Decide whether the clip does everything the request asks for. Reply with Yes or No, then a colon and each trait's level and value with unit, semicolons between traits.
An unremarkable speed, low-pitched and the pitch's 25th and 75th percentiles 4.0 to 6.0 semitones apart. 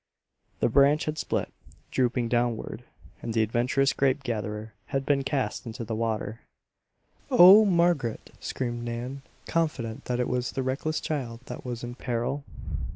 No: average, 150 wpm; low, 125 Hz; average, 3.0 semitones